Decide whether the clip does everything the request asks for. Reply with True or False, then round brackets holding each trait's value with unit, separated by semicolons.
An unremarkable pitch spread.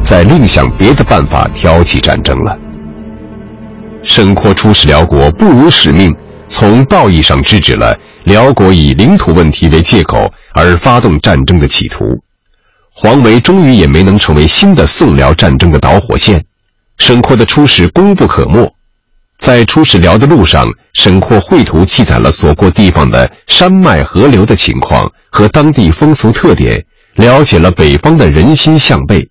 False (7.5 semitones)